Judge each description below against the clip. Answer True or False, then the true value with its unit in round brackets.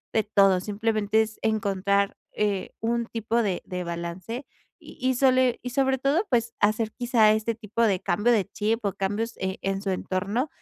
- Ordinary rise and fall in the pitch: True (3.0 semitones)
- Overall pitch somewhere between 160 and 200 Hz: False (215 Hz)